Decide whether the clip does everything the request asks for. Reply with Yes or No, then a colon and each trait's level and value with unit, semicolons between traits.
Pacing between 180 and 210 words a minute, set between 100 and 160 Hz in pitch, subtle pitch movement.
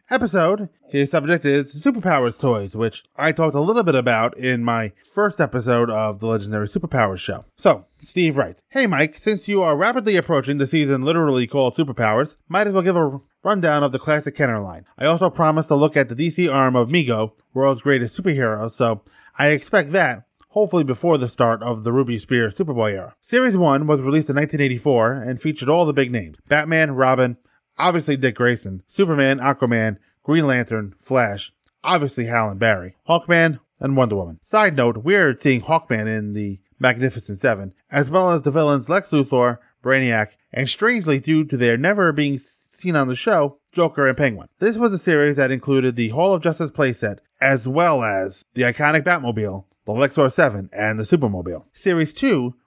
No: average, 185 wpm; low, 135 Hz; wide, 5.5 semitones